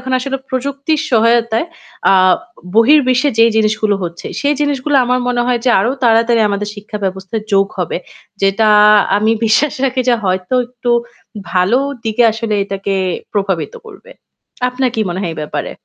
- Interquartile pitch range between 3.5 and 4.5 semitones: Yes, average, 4.2 semitones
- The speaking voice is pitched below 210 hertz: No, high, 230 Hz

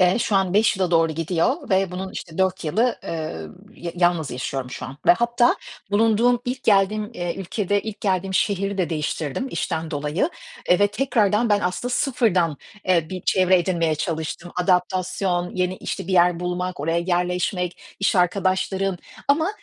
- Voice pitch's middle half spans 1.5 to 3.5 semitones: Yes, average, 2.9 semitones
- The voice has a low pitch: No, medium, 185 Hz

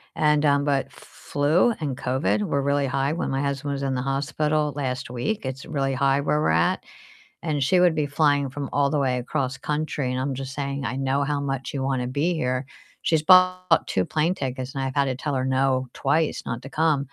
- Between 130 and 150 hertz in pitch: Yes, medium, 140 Hz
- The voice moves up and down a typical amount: No, narrow, 2.1 semitones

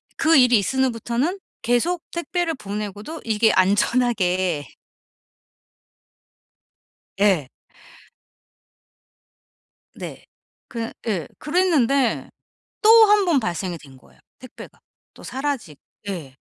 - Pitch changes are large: Yes, wide, 7.4 semitones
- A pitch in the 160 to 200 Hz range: No, high, 230 Hz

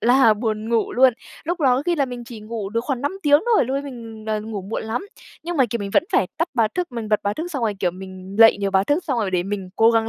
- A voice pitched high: Yes, high, 230 Hz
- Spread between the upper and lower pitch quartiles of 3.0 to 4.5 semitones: Yes, average, 4.2 semitones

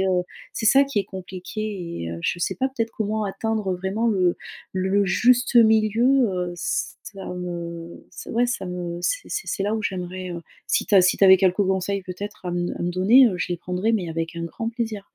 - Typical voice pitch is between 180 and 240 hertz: Yes, high, 190 Hz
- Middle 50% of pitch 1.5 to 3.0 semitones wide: No, average, 3.7 semitones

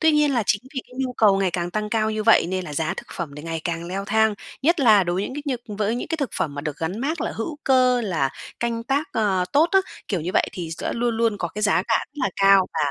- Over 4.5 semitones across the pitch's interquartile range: Yes, wide, 5.5 semitones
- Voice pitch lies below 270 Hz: Yes, high, 215 Hz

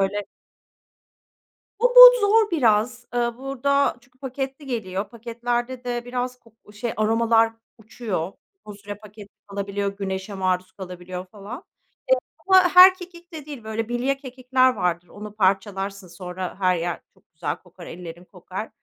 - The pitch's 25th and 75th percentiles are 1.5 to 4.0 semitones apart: No, average, 5.0 semitones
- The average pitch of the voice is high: Yes, high, 220 Hz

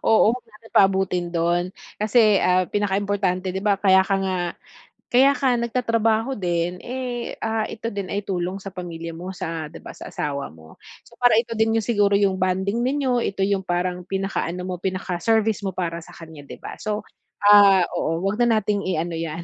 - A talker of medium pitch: No, high, 195 Hz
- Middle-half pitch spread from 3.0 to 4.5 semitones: Yes, average, 3.5 semitones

